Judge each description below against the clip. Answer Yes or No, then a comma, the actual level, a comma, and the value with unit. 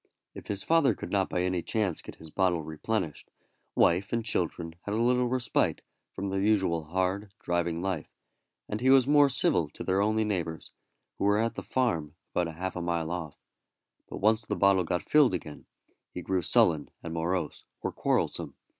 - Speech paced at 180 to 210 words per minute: Yes, average, 185 wpm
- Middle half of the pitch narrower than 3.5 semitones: No, average, 4.4 semitones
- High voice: No, very low, 95 Hz